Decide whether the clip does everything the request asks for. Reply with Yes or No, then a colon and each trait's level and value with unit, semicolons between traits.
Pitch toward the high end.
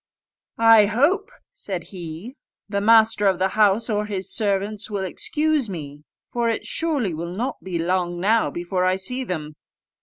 Yes: high, 205 Hz